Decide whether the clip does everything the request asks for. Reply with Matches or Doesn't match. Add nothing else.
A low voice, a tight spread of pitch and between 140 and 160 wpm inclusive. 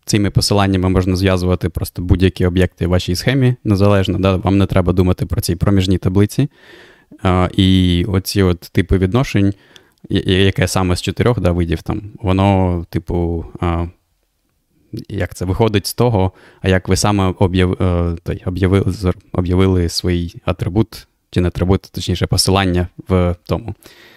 Matches